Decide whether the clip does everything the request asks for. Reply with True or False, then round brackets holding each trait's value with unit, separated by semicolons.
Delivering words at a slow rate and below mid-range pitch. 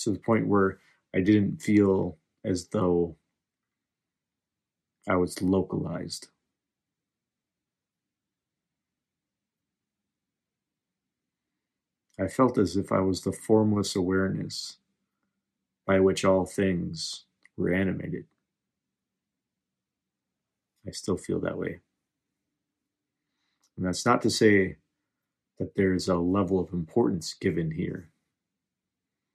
True (95 wpm; 95 Hz)